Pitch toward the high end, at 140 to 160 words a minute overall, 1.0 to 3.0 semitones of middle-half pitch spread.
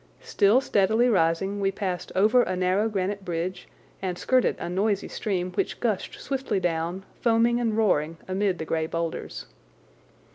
No: high, 195 Hz; average, 150 wpm; average, 3.5 semitones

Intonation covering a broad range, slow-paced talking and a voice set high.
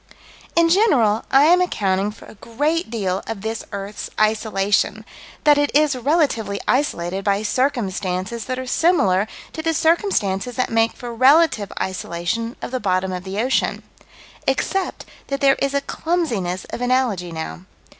No: wide, 6.4 semitones; average, 155 wpm; high, 230 Hz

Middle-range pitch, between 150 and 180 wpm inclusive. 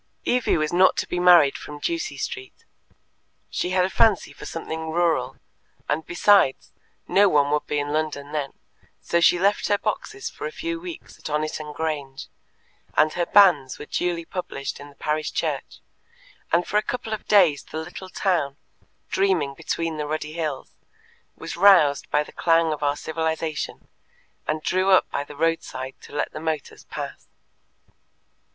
Yes: medium, 160 Hz; average, 170 wpm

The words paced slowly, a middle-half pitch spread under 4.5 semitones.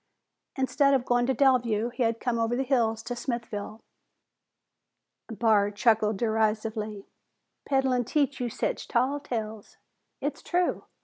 Yes: slow, 130 wpm; average, 3.1 semitones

